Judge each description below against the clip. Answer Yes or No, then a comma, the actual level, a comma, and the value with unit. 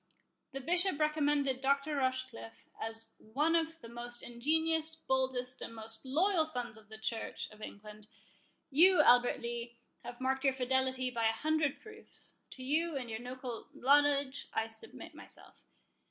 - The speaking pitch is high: Yes, very high, 260 Hz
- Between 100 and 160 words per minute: Yes, average, 155 wpm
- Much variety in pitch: No, average, 4.1 semitones